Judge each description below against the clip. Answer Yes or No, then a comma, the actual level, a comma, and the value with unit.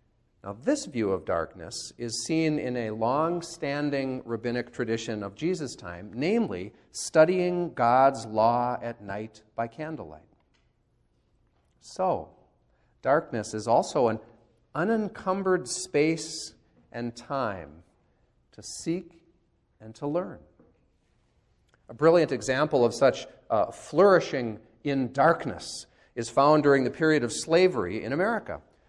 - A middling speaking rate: No, slow, 115 wpm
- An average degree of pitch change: No, wide, 6.0 semitones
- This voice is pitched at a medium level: No, low, 130 Hz